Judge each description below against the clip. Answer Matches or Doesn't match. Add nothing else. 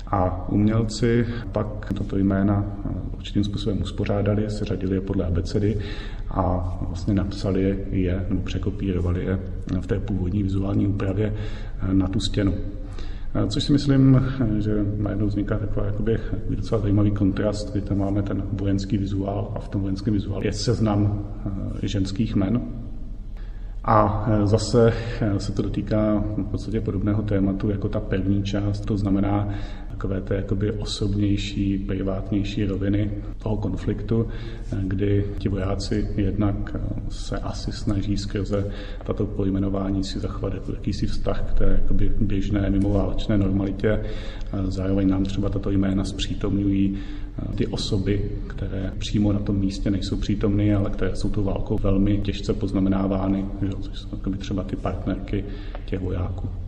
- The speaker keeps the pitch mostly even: Matches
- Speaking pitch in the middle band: Doesn't match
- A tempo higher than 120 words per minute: Matches